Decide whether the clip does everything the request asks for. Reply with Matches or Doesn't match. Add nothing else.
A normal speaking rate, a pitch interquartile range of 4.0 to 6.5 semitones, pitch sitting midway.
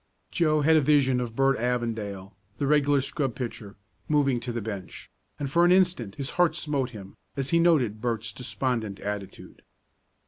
Doesn't match